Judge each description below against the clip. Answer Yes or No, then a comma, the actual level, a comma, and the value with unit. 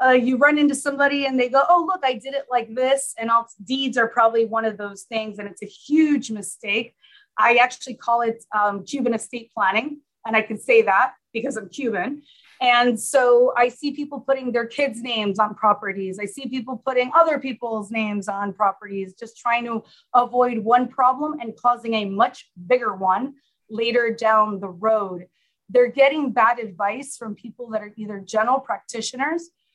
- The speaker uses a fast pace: No, average, 185 wpm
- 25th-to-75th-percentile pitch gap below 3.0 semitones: No, average, 3.5 semitones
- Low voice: No, high, 235 Hz